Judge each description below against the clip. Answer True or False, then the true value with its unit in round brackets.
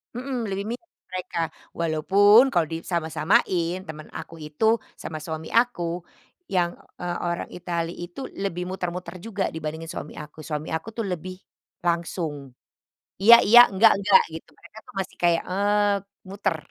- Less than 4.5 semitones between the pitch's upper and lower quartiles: True (3.5 semitones)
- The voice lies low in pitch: False (175 Hz)